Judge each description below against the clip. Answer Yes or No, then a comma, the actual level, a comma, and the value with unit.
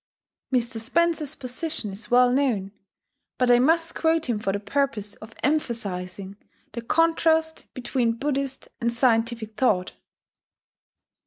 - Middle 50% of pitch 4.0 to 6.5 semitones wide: Yes, average, 4.7 semitones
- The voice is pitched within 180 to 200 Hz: No, high, 245 Hz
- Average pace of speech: No, slow, 120 wpm